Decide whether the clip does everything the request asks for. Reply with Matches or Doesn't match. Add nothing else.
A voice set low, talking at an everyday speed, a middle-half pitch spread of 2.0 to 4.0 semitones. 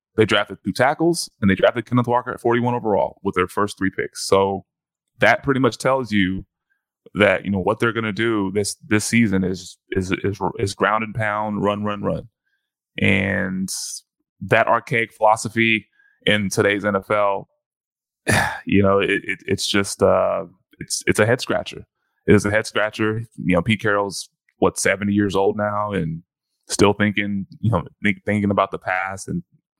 Matches